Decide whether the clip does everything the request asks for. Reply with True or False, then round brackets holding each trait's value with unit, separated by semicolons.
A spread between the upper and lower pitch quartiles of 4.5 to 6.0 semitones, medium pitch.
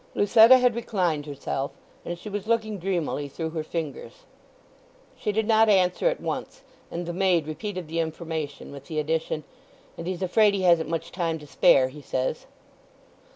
True (4.8 semitones; 170 Hz)